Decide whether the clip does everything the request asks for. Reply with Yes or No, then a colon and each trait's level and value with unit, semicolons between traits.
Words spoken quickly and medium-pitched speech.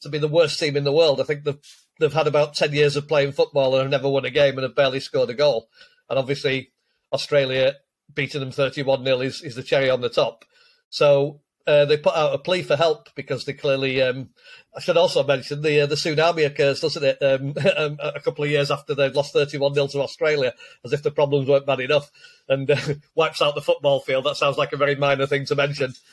Yes: fast, 235 wpm; medium, 145 Hz